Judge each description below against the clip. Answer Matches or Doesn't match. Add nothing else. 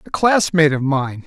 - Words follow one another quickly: Doesn't match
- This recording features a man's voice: Matches